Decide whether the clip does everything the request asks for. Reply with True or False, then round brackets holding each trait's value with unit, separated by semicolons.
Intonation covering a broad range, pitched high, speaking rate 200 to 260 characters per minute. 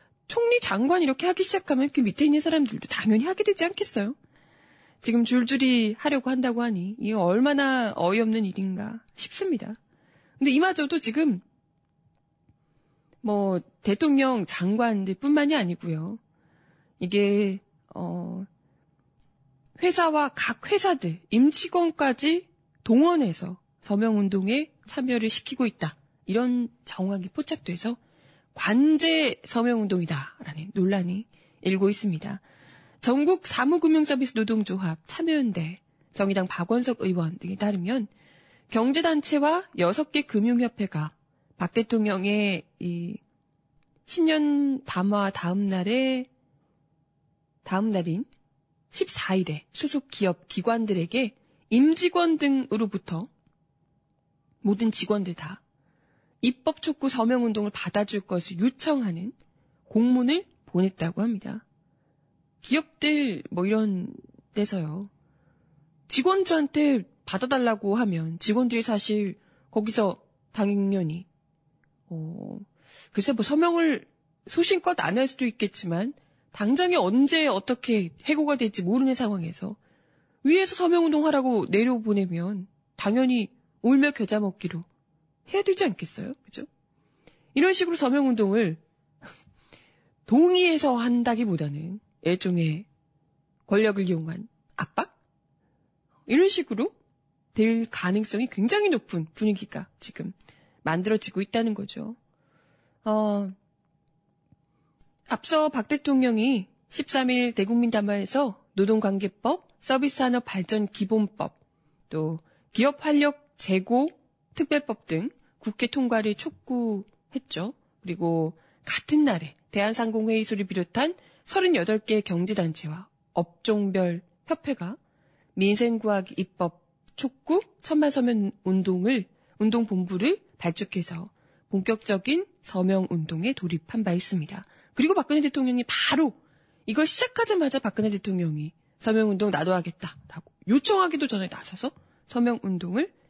True (6.9 semitones; 215 Hz; 250 characters per minute)